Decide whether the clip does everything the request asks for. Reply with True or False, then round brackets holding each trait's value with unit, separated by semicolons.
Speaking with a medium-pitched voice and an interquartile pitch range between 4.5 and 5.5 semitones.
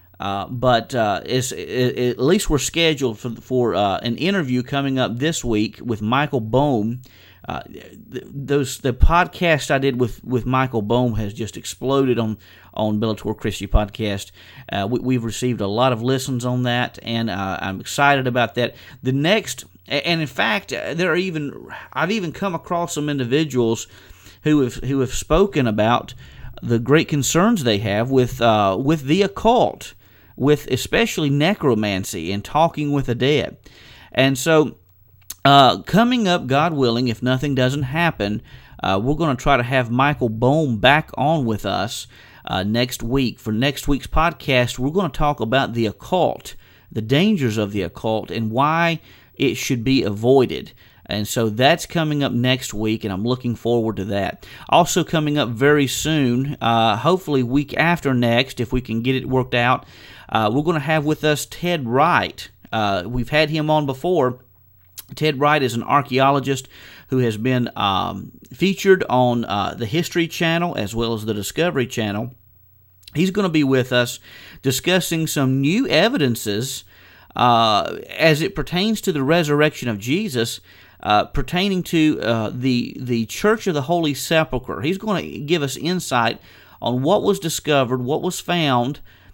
False (130 Hz; 4.8 semitones)